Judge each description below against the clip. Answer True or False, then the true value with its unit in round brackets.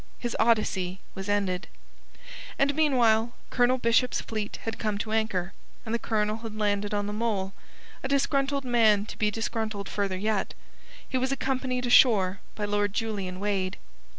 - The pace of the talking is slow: False (155 wpm)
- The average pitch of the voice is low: False (215 Hz)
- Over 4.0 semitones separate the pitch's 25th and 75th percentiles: False (2.9 semitones)